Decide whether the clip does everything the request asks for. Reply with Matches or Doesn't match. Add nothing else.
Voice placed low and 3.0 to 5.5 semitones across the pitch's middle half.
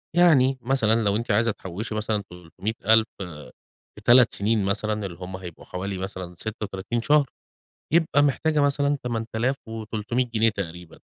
Matches